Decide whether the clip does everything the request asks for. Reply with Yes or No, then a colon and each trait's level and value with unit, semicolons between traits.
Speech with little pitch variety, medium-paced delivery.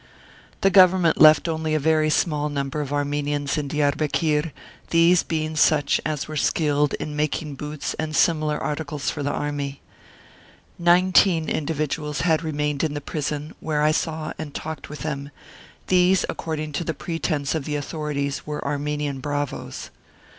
Yes: narrow, 1.5 semitones; average, 155 wpm